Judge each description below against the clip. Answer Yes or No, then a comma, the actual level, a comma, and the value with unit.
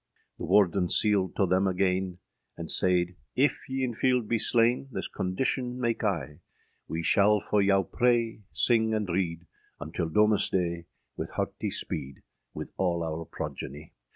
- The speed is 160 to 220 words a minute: No, average, 150 wpm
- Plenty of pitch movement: No, average, 4.5 semitones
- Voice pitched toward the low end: Yes, very low, 95 Hz